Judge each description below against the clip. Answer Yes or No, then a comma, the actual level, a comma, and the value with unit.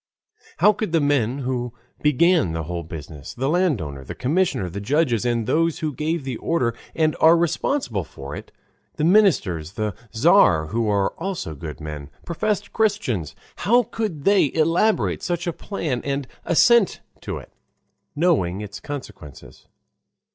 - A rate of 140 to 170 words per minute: Yes, average, 150 wpm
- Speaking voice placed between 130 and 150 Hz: Yes, medium, 140 Hz